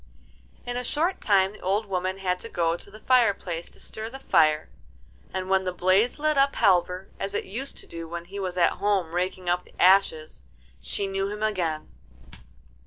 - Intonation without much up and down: No, average, 3.0 semitones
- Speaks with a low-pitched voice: No, high, 190 Hz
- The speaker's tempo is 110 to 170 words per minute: No, average, 195 wpm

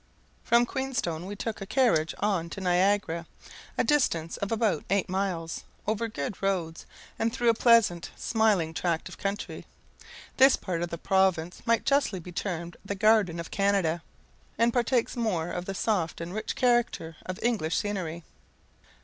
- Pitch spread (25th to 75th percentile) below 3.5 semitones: No, average, 4.9 semitones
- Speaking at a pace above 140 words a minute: Yes, average, 160 wpm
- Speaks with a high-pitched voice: Yes, high, 195 Hz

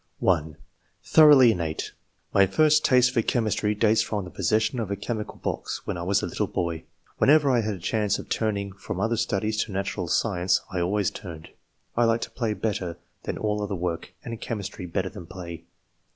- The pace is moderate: Yes, average, 195 wpm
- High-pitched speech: No, low, 105 Hz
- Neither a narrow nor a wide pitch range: Yes, average, 3.9 semitones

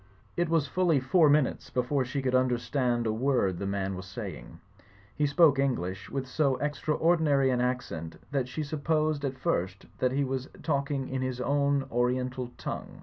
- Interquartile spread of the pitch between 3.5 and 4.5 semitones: No, average, 2.7 semitones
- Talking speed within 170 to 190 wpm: Yes, average, 175 wpm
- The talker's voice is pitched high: No, low, 130 Hz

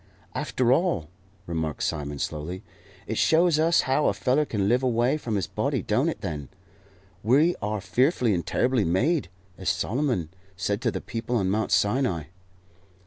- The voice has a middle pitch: No, low, 115 Hz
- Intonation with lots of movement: Yes, wide, 6.1 semitones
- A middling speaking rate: Yes, average, 160 wpm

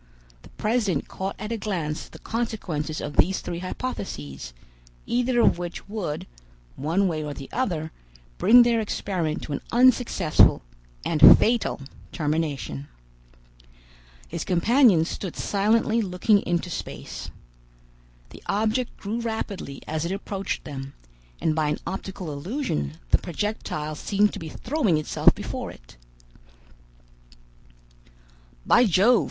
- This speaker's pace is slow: Yes, slow, 125 wpm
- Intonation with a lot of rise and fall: Yes, wide, 6.2 semitones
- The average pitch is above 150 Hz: Yes, medium, 185 Hz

